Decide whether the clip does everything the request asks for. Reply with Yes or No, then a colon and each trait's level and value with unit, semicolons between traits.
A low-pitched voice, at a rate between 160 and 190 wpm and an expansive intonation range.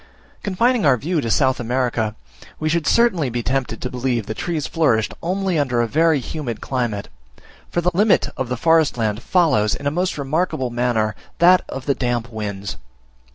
Yes: low, 130 Hz; average, 180 wpm; wide, 5.8 semitones